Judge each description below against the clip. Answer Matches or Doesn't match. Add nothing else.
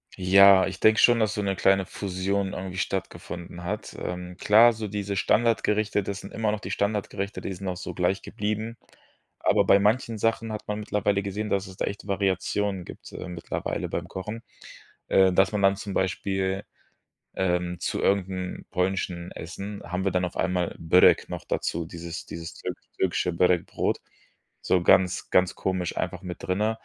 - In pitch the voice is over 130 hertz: Doesn't match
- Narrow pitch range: Matches